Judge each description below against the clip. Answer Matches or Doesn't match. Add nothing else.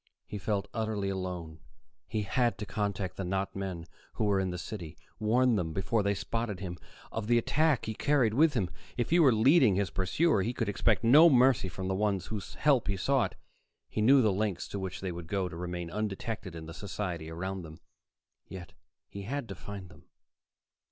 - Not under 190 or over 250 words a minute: Matches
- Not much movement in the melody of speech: Doesn't match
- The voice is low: Matches